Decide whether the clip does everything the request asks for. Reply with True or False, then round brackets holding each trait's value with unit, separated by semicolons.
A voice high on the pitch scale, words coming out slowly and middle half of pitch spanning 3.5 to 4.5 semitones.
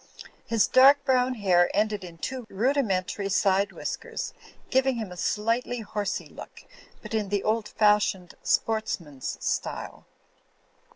True (210 Hz; 130 wpm; 4.0 semitones)